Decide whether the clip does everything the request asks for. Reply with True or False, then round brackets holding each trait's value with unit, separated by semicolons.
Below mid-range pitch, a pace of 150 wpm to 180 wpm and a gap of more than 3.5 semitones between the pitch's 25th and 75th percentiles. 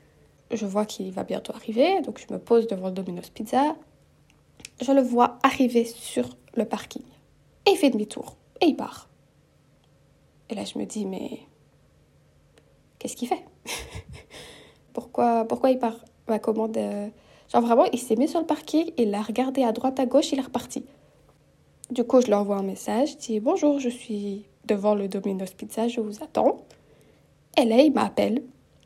False (235 Hz; 175 wpm; 4.4 semitones)